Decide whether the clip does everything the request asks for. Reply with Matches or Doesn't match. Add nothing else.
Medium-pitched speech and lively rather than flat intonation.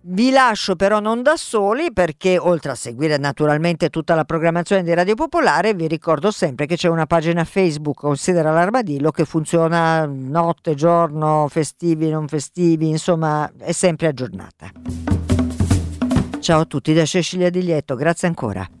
Doesn't match